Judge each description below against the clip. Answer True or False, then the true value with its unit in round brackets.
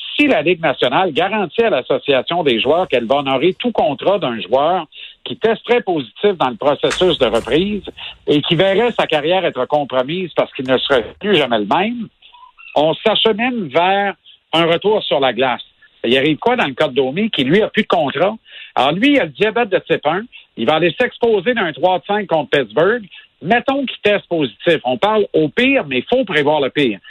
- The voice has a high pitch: True (195 Hz)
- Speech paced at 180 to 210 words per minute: True (205 wpm)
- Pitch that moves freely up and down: True (6.9 semitones)